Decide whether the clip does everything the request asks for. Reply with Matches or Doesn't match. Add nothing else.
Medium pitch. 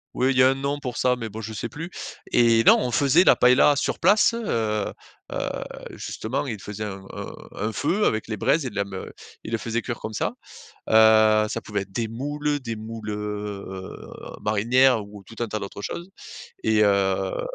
Doesn't match